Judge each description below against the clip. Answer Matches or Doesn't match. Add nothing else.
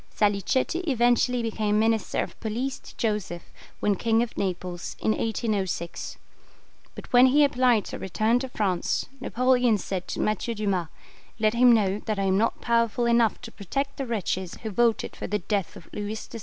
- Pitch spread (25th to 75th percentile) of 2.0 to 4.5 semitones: Matches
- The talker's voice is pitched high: Matches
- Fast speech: Doesn't match